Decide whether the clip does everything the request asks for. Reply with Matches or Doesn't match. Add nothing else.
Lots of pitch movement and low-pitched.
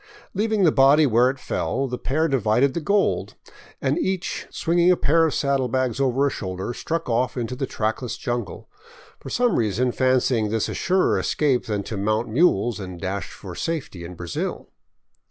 Matches